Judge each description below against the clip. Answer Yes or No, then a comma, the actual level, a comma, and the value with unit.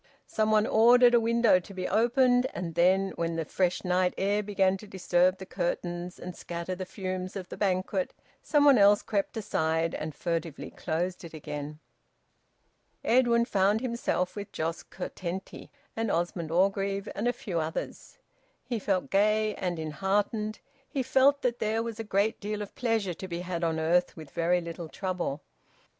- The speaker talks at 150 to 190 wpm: Yes, average, 170 wpm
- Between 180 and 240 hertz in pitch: Yes, high, 190 Hz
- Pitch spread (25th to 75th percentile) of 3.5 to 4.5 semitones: Yes, average, 3.8 semitones